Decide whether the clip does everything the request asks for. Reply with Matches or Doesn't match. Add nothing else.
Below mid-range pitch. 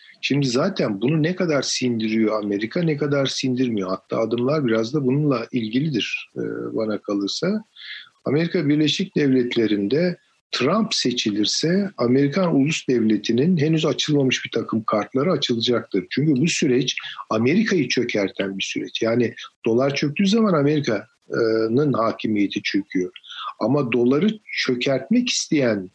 Matches